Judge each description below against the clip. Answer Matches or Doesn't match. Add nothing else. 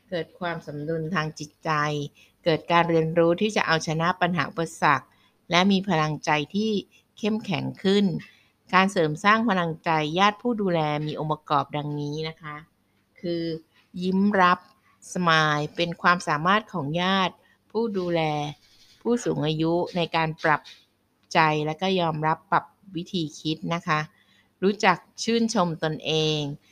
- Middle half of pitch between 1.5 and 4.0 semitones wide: Matches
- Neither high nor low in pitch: Matches